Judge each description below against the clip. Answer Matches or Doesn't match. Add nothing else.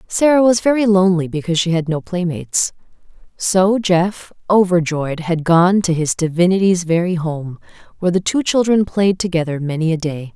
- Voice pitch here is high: Doesn't match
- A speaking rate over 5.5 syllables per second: Doesn't match